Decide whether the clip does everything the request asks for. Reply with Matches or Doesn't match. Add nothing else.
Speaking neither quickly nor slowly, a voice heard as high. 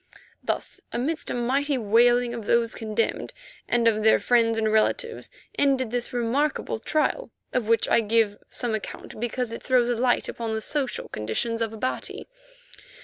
Matches